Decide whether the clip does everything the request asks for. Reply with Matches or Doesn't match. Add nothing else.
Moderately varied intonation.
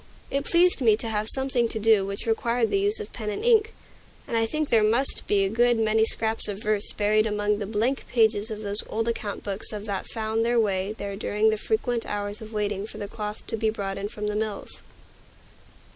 Doesn't match